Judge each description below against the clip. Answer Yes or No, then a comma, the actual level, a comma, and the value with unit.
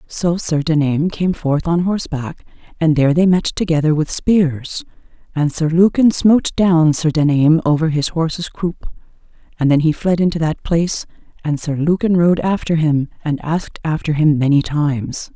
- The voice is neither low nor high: Yes, medium, 160 Hz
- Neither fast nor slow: Yes, average, 170 wpm